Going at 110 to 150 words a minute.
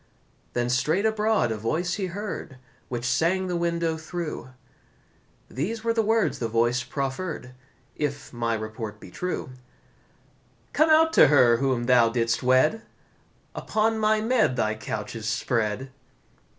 Yes: average, 140 wpm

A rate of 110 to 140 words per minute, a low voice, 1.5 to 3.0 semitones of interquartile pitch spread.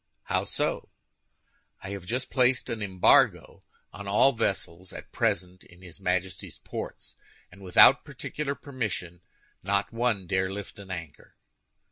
No: slow, 135 wpm; low, 100 Hz; average, 3.9 semitones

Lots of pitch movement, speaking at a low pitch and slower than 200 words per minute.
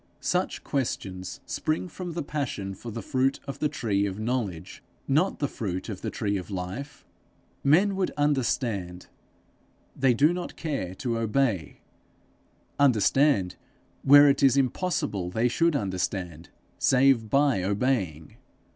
Yes: wide, 6.7 semitones; low, 125 Hz; slow, 135 wpm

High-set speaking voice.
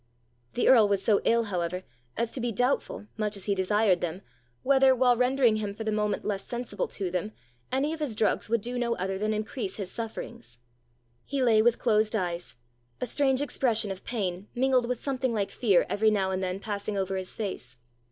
Yes: high, 215 Hz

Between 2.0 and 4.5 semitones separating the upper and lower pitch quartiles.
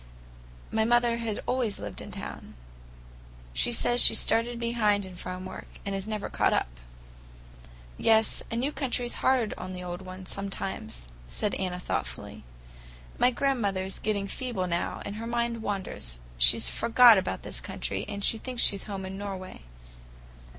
Yes: average, 4.0 semitones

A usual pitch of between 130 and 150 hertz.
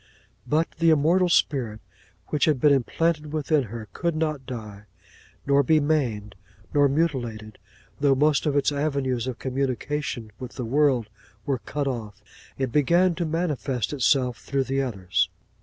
Yes: medium, 140 Hz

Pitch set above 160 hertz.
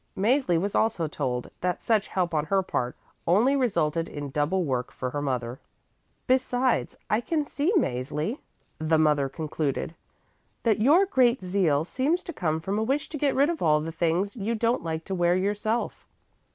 Yes: medium, 185 Hz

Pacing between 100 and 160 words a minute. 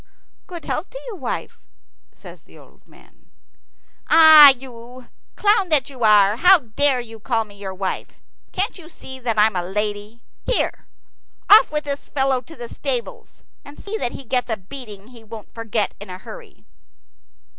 No: average, 170 wpm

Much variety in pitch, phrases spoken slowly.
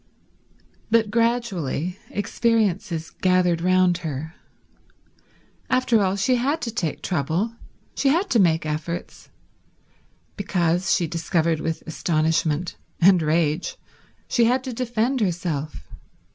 Yes: wide, 5.9 semitones; slow, 110 wpm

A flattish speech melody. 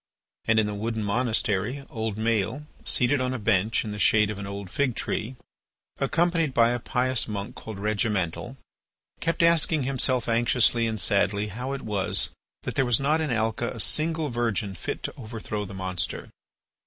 No: average, 3.7 semitones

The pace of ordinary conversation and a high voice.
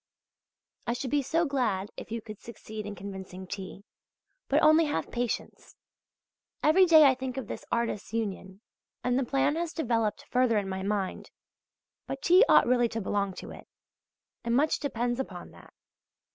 Yes: average, 170 wpm; high, 235 Hz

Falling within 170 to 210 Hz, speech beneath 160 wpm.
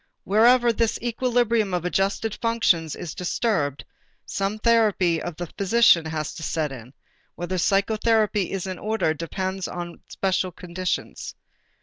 Yes: high, 190 Hz; slow, 135 wpm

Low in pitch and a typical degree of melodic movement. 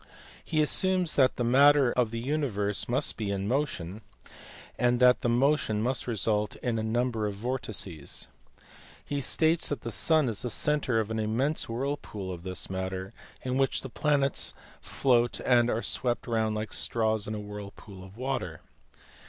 Yes: low, 120 Hz; average, 4.2 semitones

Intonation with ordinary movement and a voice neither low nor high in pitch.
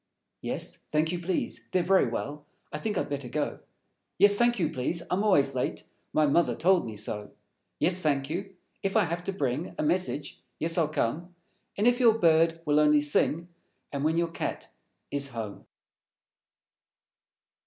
Yes: average, 4.1 semitones; medium, 165 Hz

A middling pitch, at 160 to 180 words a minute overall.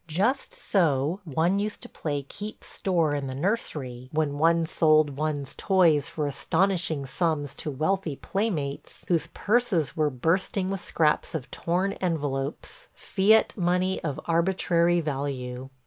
No: medium, 160 Hz; average, 140 wpm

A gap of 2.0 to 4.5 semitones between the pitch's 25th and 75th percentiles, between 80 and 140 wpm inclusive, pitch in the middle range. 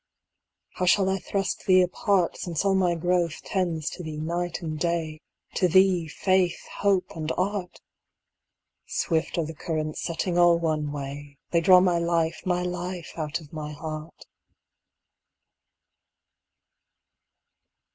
Yes: narrow, 2.5 semitones; slow, 135 wpm; medium, 170 Hz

